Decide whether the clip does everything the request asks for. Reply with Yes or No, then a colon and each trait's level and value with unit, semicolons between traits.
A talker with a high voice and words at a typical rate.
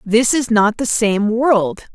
Yes: high, 230 Hz; average, 185 wpm